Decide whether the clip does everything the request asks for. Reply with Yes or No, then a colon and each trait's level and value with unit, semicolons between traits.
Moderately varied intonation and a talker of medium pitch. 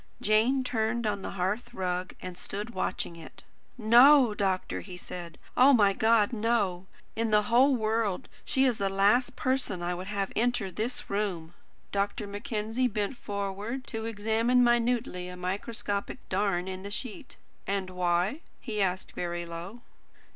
No: average, 4.0 semitones; high, 210 Hz